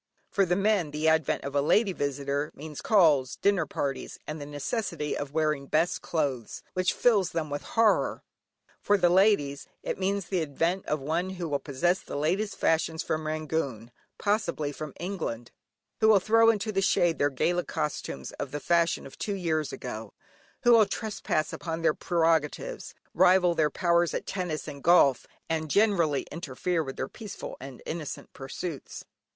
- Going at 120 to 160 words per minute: No, average, 170 wpm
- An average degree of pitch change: Yes, average, 4.5 semitones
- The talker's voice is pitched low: No, medium, 165 Hz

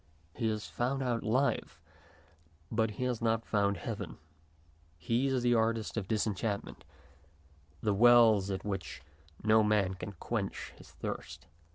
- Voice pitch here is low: Yes, low, 110 Hz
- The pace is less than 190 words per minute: Yes, average, 140 wpm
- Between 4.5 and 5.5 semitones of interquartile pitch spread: No, average, 2.8 semitones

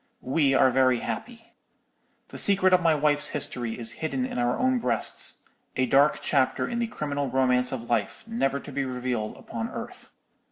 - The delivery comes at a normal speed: Yes, average, 170 wpm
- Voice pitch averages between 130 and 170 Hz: Yes, low, 135 Hz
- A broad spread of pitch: No, average, 4.1 semitones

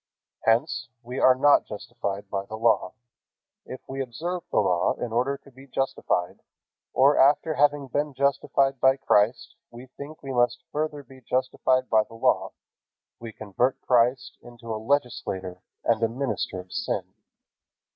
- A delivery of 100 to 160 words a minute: Yes, average, 155 wpm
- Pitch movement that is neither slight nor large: Yes, average, 3.5 semitones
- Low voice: Yes, low, 125 Hz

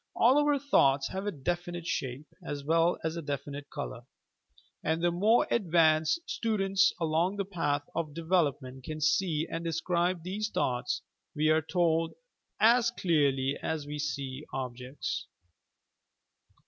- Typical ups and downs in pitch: Yes, average, 4.1 semitones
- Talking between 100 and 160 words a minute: Yes, average, 145 wpm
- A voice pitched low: No, medium, 160 Hz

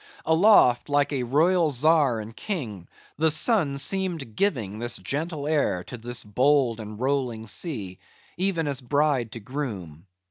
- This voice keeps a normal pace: Yes, average, 145 wpm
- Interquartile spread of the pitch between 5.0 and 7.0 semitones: Yes, wide, 5.6 semitones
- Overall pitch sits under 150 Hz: Yes, low, 135 Hz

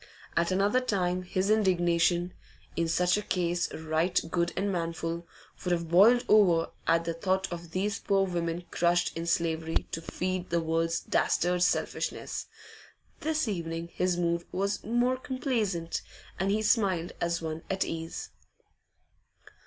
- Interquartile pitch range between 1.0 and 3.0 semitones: Yes, narrow, 2.6 semitones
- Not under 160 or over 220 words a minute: No, average, 145 wpm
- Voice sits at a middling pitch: Yes, medium, 175 Hz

